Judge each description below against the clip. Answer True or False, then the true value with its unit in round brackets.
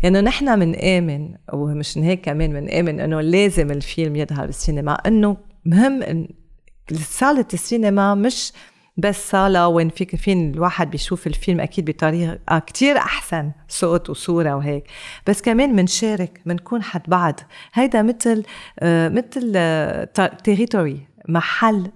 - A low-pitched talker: False (180 Hz)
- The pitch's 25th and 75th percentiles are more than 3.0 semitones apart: True (4.2 semitones)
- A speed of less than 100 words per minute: False (130 wpm)